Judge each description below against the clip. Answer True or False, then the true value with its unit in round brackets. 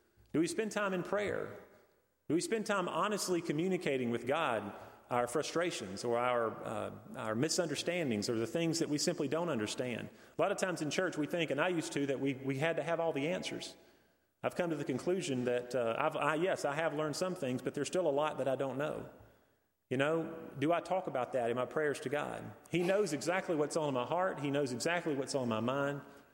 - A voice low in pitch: False (150 Hz)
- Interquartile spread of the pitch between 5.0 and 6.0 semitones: False (4.6 semitones)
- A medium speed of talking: False (230 wpm)